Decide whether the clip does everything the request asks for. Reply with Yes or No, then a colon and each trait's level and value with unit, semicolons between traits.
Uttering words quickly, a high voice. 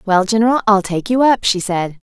Yes: fast, 225 wpm; high, 205 Hz